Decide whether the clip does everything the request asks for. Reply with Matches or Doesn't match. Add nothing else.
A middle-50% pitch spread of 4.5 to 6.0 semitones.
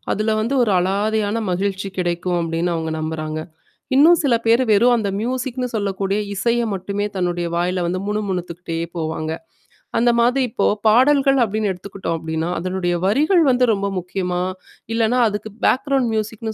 Matches